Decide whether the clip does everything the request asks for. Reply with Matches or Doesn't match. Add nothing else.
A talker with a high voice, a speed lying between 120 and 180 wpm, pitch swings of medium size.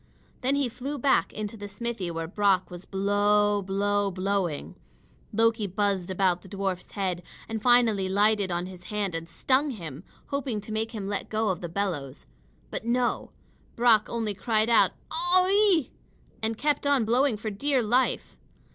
Matches